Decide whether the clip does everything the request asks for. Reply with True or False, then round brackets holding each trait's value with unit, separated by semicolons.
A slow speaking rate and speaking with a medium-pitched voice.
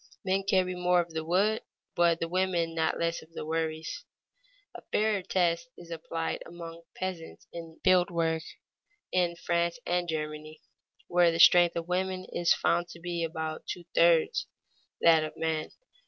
False (160 wpm; 170 Hz)